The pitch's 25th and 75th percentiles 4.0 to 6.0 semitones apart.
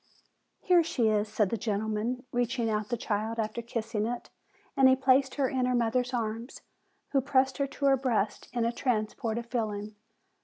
No: average, 3.1 semitones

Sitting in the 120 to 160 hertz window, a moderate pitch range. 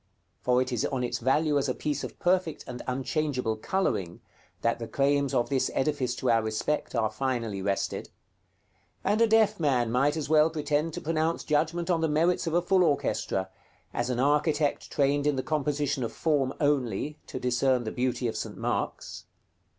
Yes: medium, 140 Hz; average, 3.8 semitones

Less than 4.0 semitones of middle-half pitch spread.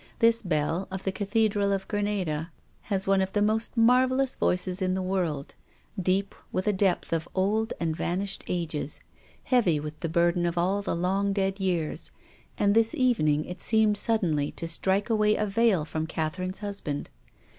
Yes: average, 3.5 semitones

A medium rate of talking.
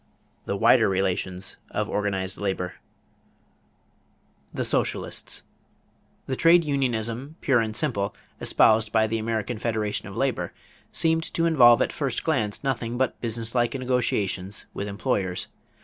No: slow, 125 wpm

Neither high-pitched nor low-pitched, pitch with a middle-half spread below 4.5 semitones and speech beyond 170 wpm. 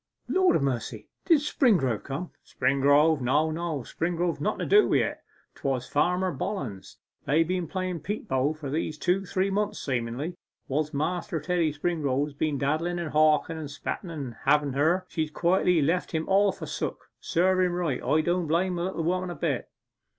Yes: medium, 160 Hz; average, 4.0 semitones; average, 185 wpm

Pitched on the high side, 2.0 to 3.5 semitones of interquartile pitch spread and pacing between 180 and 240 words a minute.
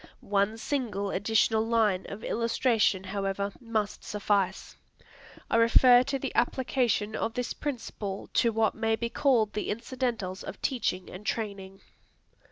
No: high, 220 Hz; average, 2.9 semitones; slow, 135 wpm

